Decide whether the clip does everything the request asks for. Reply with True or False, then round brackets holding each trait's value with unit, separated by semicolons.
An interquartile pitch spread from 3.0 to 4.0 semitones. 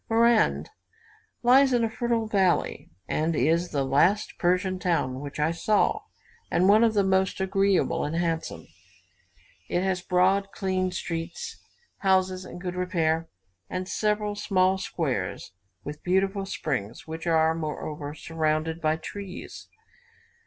True (3.4 semitones)